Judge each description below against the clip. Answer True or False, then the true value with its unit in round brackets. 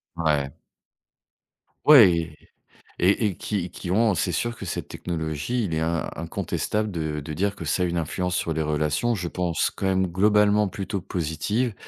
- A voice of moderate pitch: False (90 Hz)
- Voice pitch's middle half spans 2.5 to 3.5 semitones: False (4.2 semitones)